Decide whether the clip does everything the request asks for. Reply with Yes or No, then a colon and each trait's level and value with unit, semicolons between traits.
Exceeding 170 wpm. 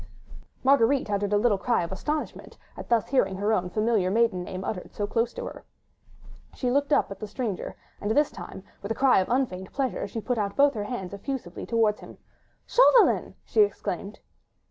Yes: average, 190 wpm